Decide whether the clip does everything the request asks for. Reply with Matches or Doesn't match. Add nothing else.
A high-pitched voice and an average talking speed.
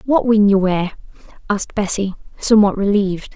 Matches